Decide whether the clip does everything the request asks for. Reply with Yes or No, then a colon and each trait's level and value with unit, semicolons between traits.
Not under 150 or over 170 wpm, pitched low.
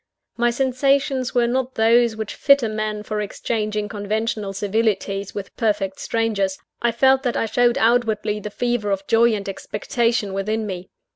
No: average, 160 wpm; high, 220 Hz